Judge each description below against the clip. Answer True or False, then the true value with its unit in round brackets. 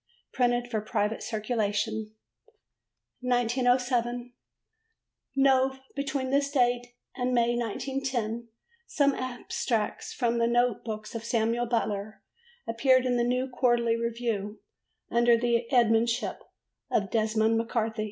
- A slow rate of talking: True (110 wpm)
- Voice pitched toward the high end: True (240 Hz)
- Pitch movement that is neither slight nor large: False (1.9 semitones)